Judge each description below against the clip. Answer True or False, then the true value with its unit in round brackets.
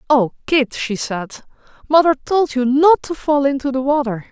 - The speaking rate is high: False (180 wpm)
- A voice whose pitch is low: False (275 Hz)